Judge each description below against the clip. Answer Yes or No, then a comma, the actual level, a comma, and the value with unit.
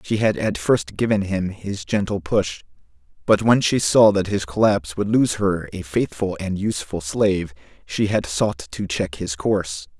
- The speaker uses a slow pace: No, average, 185 wpm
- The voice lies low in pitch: Yes, low, 100 Hz